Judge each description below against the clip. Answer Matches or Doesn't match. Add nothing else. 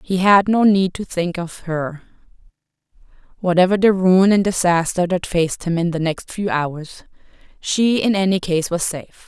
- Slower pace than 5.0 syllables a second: Matches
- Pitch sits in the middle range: Matches